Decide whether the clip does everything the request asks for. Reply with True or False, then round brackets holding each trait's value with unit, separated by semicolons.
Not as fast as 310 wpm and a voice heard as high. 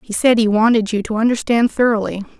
True (200 wpm; 220 Hz)